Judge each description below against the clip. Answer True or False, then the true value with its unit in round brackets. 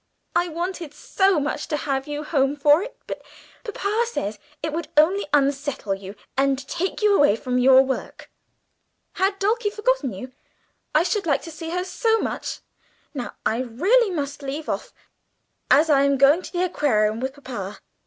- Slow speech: False (175 wpm)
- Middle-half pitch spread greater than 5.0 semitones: True (5.5 semitones)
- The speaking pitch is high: True (295 Hz)